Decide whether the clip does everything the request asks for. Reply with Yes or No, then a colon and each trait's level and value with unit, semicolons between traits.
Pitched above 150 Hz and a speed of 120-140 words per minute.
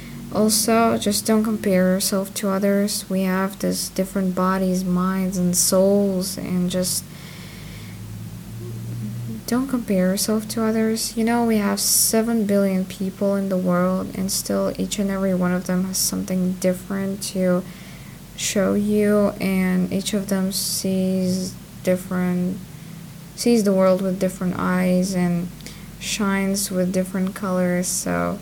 Yes: medium, 185 Hz; slow, 135 wpm